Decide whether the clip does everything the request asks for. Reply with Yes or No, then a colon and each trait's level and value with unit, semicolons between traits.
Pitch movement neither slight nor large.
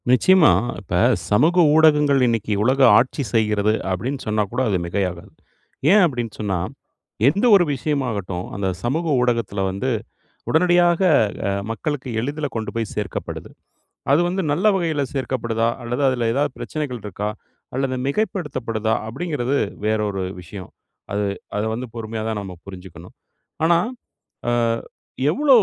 No: wide, 5.8 semitones